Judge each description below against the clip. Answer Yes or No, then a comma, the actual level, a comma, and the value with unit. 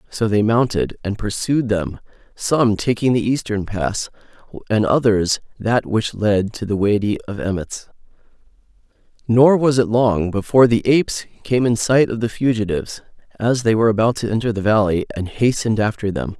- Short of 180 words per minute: Yes, average, 170 wpm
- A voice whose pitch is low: Yes, low, 110 Hz